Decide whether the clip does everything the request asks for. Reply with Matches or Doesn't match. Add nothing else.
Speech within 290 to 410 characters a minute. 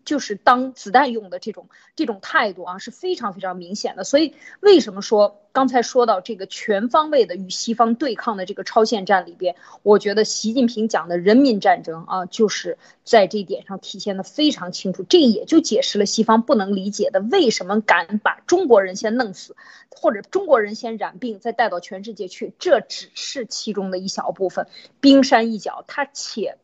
Matches